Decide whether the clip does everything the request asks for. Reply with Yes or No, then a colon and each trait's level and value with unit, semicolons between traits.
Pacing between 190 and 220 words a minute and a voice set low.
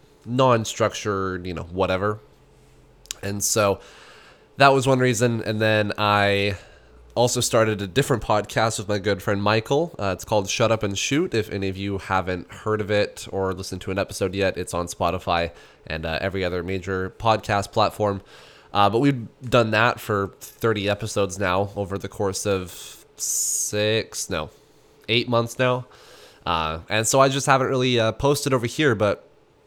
No: average, 170 wpm; low, 105 Hz